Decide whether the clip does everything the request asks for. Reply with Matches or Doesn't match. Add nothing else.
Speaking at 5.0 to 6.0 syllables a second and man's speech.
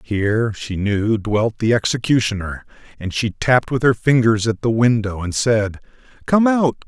Doesn't match